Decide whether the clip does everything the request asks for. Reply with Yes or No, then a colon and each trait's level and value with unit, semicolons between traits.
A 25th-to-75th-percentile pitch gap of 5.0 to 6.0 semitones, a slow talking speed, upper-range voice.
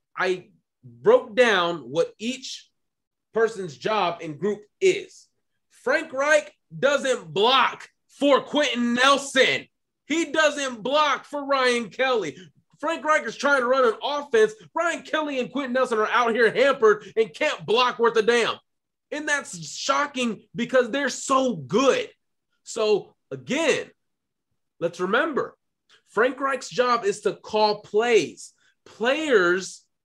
Yes: wide, 5.4 semitones; slow, 130 wpm; very high, 255 Hz